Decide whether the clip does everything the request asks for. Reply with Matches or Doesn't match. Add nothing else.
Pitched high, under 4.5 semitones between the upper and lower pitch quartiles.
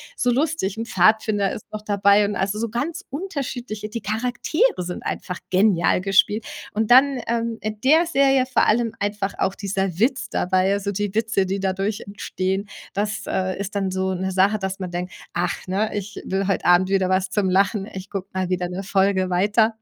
Matches